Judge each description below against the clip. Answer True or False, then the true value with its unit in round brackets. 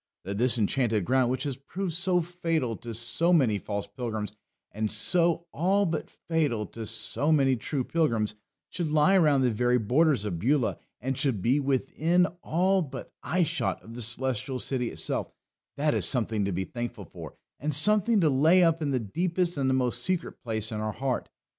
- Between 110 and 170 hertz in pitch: True (135 Hz)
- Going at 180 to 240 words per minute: True (190 wpm)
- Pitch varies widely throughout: True (6.1 semitones)